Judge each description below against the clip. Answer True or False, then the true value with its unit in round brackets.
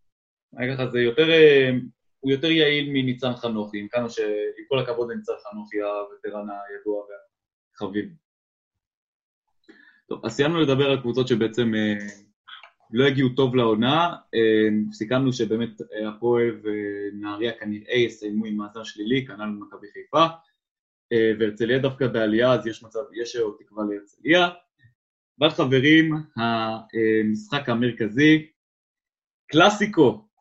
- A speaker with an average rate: True (110 wpm)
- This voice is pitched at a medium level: False (120 Hz)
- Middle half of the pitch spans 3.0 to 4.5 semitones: True (4.2 semitones)